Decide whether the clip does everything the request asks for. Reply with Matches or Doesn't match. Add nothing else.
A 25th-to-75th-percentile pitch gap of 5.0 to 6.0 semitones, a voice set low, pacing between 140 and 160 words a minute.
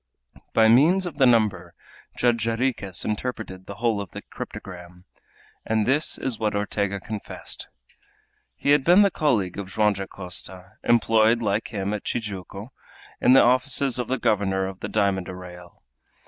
Doesn't match